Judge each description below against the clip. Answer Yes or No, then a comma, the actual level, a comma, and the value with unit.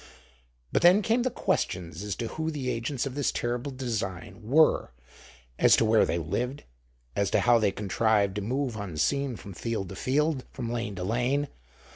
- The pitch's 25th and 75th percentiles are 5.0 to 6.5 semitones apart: Yes, wide, 5.4 semitones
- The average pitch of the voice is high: No, low, 115 Hz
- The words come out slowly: No, average, 180 wpm